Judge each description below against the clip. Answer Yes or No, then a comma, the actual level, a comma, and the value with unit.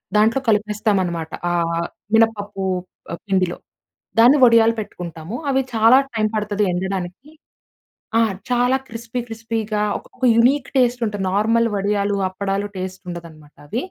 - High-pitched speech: Yes, high, 210 Hz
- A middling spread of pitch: Yes, average, 3.5 semitones